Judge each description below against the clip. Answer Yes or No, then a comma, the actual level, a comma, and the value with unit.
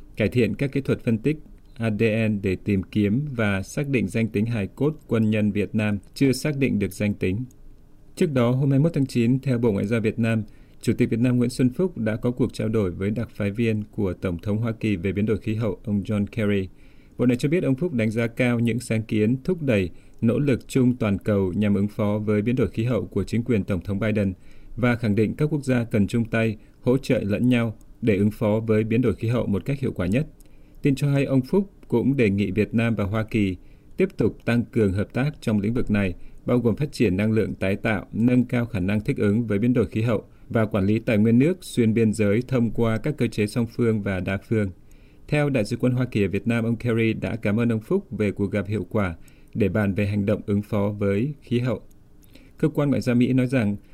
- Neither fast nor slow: No, fast, 255 wpm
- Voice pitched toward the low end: Yes, low, 115 Hz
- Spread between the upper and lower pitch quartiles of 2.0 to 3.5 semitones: Yes, average, 3.2 semitones